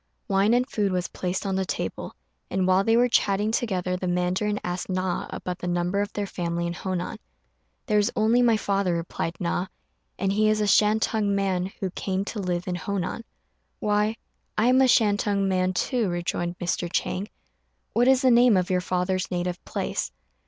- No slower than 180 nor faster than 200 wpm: Yes, average, 190 wpm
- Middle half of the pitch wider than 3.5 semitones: No, average, 2.8 semitones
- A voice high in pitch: Yes, high, 195 Hz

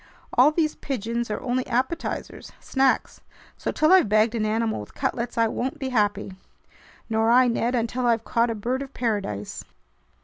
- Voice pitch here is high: Yes, high, 235 Hz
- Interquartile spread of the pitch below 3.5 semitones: Yes, average, 2.7 semitones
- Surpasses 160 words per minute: Yes, average, 170 wpm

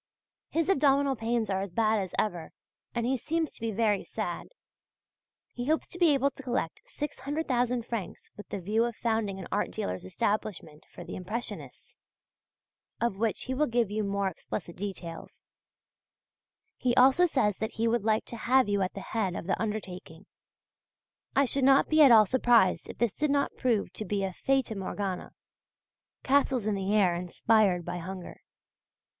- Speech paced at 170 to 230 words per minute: Yes, average, 175 wpm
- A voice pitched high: Yes, high, 220 Hz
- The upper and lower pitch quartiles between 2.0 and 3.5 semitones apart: No, average, 4.8 semitones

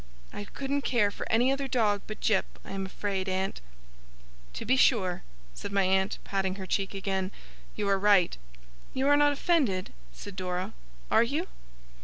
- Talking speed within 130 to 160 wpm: No, average, 170 wpm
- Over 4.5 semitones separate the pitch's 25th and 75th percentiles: Yes, average, 4.9 semitones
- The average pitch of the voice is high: Yes, high, 200 Hz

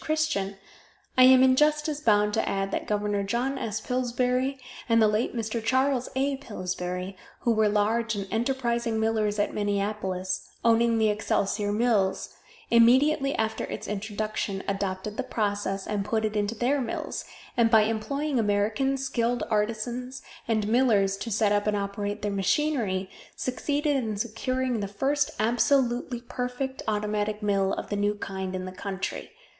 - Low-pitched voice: No, high, 220 Hz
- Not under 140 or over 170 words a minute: Yes, average, 155 wpm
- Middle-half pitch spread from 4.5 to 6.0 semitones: No, average, 3.5 semitones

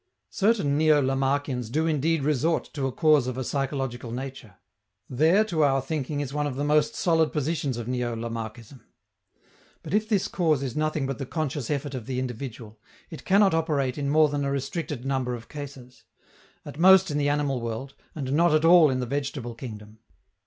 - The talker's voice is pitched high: No, medium, 140 Hz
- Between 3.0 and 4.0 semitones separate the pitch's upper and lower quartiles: Yes, average, 3.4 semitones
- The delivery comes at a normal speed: Yes, average, 190 wpm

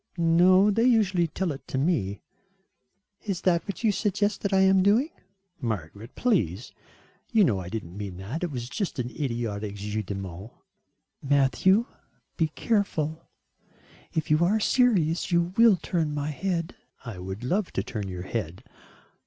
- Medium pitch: Yes, medium, 160 Hz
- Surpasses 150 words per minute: Yes, average, 160 wpm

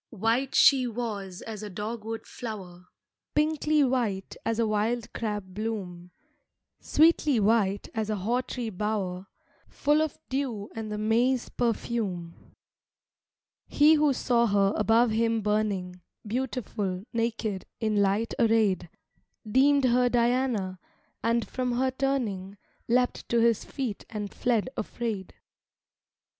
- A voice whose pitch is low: No, high, 225 Hz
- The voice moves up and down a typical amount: Yes, average, 3.3 semitones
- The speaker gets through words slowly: Yes, slow, 125 wpm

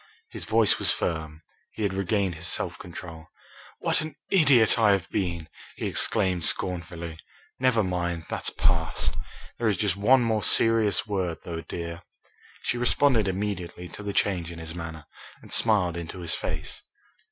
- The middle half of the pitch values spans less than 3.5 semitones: No, average, 4.2 semitones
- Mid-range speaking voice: No, very low, 90 Hz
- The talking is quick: No, average, 160 wpm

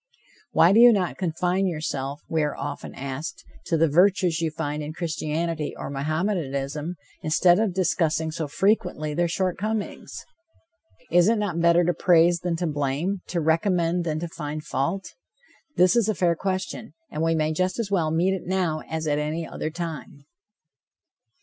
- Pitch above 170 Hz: No, medium, 165 Hz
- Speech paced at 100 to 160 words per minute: No, average, 170 wpm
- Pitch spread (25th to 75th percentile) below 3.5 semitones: Yes, average, 2.9 semitones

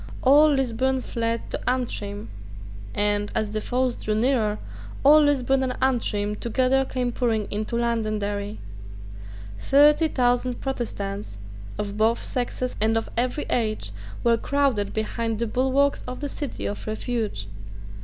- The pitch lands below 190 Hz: No, high, 235 Hz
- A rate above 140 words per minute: No, slow, 135 wpm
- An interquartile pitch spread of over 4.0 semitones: No, average, 3.5 semitones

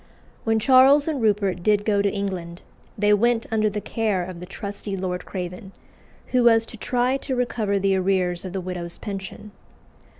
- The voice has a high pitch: Yes, high, 205 Hz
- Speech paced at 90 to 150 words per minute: No, average, 175 wpm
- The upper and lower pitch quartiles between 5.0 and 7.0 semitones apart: No, average, 3.3 semitones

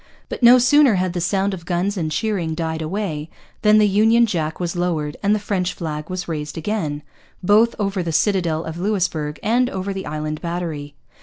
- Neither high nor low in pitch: Yes, medium, 180 Hz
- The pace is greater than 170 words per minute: Yes, average, 190 wpm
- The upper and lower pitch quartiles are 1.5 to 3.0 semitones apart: No, average, 4.5 semitones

